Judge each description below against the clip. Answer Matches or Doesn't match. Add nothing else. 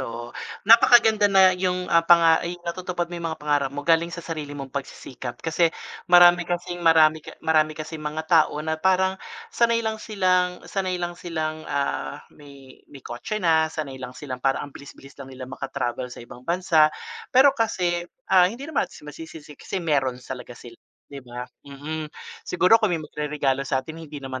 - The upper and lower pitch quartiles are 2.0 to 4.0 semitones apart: Doesn't match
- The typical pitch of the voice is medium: Matches